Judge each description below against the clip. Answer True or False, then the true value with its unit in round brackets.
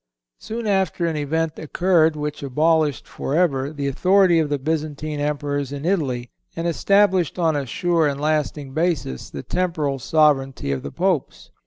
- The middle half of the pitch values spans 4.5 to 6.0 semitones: False (3.2 semitones)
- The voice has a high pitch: False (155 Hz)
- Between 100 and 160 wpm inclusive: True (155 wpm)